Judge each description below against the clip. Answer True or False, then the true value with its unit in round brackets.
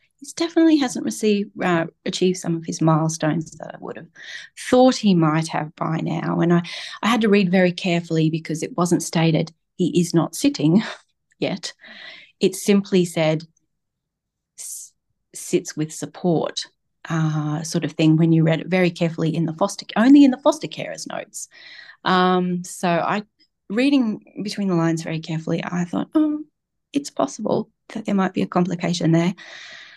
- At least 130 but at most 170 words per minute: True (165 wpm)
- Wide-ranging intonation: False (4.0 semitones)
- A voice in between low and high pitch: True (175 Hz)